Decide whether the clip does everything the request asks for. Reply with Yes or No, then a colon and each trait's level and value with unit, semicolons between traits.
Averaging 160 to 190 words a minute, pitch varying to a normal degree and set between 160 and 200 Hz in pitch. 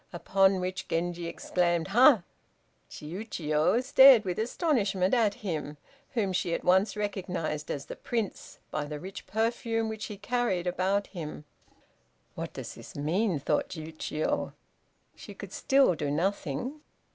No: slow, 135 wpm; average, 4.9 semitones; medium, 185 Hz